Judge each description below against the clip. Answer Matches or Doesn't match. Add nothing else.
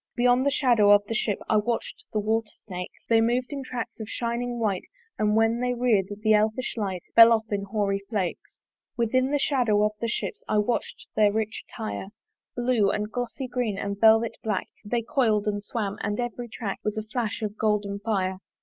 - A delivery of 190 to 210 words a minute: Matches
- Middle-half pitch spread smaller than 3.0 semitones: Matches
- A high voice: Matches